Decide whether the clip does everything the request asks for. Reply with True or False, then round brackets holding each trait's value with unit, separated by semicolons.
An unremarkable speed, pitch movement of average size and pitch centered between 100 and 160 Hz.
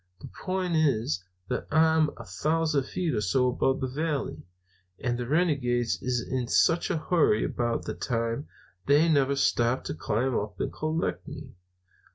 True (170 wpm; 4.7 semitones; 135 Hz)